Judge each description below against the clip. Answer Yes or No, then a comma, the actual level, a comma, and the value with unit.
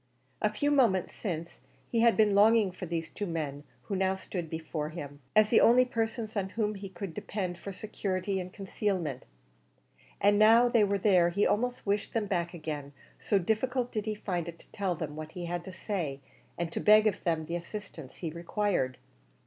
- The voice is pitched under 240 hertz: Yes, high, 190 Hz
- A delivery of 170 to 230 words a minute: Yes, average, 200 wpm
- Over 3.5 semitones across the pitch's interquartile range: Yes, average, 4.0 semitones